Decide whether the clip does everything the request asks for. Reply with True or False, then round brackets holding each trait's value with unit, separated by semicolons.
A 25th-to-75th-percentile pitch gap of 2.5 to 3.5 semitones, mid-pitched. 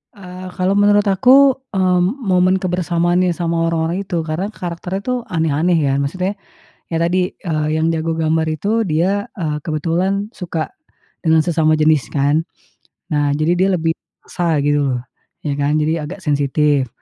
True (3.0 semitones; 170 Hz)